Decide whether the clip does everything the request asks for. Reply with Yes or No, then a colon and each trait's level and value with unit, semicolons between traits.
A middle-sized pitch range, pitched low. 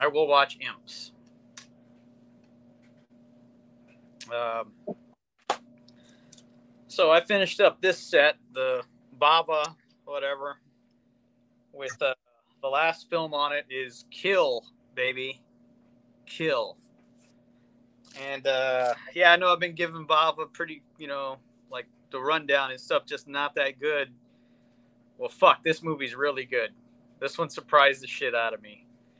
Yes: average, 3.4 semitones; low, 120 Hz